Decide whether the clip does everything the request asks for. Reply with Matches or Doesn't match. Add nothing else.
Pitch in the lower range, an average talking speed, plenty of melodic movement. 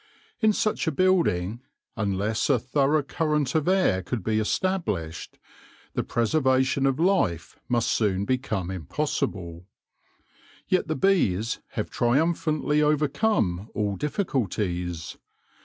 Doesn't match